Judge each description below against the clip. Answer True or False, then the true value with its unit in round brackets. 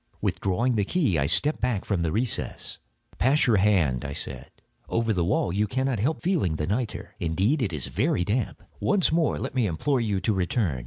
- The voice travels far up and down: True (6.4 semitones)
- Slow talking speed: False (200 wpm)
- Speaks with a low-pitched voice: True (105 Hz)